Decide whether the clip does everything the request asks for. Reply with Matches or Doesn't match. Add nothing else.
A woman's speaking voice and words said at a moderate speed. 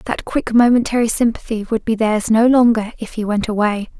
Matches